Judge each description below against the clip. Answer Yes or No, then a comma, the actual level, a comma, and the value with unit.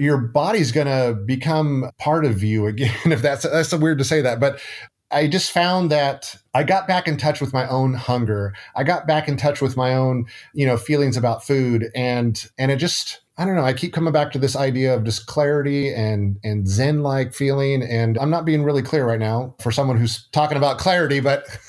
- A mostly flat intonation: No, average, 3.6 semitones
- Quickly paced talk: Yes, fast, 225 wpm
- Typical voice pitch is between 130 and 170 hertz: Yes, medium, 140 Hz